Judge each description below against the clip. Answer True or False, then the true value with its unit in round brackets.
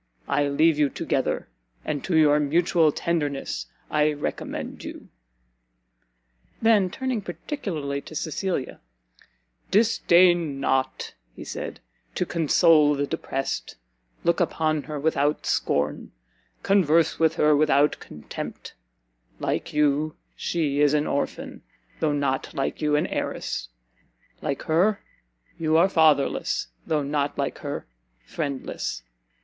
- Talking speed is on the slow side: True (115 wpm)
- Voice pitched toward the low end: False (150 Hz)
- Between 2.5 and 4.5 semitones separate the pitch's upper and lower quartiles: True (2.9 semitones)